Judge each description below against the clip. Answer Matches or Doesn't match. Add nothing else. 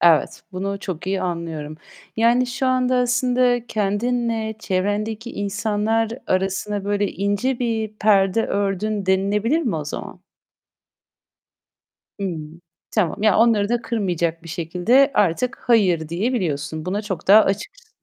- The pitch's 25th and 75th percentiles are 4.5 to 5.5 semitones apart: Doesn't match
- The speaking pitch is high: Matches